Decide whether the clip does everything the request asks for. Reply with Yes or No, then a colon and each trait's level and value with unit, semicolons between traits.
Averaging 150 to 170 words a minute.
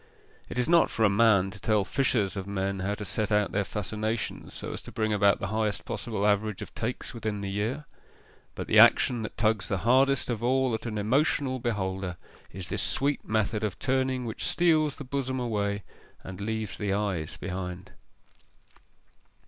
No: average, 185 wpm